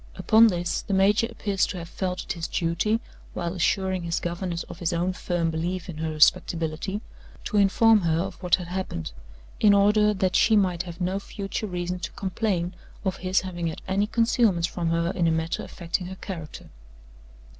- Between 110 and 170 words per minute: No, average, 190 wpm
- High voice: No, medium, 180 Hz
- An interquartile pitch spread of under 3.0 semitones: Yes, narrow, 2.5 semitones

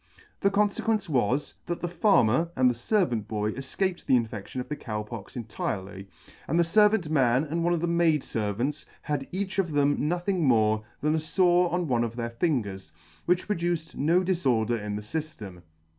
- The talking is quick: No, average, 190 wpm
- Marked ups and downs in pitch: Yes, wide, 7.0 semitones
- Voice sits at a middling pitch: Yes, medium, 145 Hz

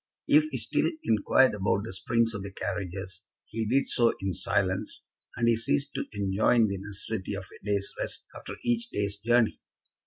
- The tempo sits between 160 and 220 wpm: Yes, average, 180 wpm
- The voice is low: Yes, low, 105 Hz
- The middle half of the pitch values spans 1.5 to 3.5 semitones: Yes, average, 3.1 semitones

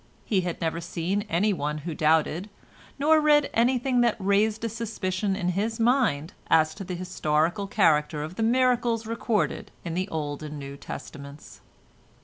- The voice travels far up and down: Yes, wide, 6.2 semitones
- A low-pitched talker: No, high, 190 Hz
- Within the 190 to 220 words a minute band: No, average, 155 wpm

